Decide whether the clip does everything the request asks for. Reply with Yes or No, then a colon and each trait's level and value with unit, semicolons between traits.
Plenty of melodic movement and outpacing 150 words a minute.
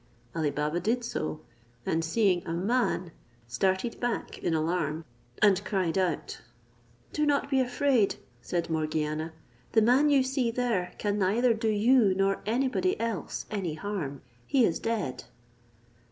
No: wide, 6.4 semitones; average, 145 wpm